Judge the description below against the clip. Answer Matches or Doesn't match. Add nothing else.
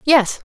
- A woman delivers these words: Matches